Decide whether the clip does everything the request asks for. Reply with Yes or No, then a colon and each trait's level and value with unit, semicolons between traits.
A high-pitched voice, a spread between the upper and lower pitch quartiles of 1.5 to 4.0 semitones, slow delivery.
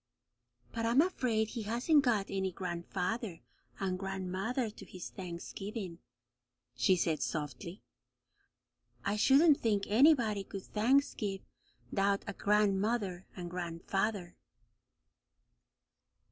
Yes: high, 200 Hz; average, 3.7 semitones; slow, 100 wpm